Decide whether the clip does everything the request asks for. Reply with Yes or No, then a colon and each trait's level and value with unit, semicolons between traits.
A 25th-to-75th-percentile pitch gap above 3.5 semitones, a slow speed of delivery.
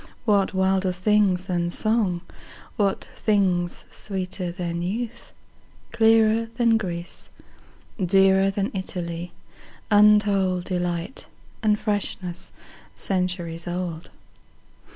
No: average, 2.9 semitones; slow, 75 wpm